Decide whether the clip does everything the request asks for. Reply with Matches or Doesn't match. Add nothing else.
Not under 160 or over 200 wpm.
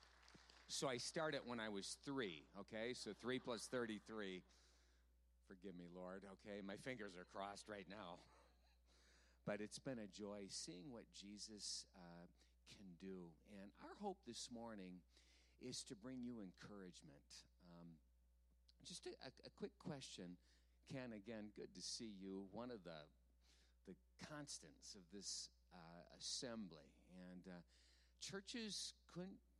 Doesn't match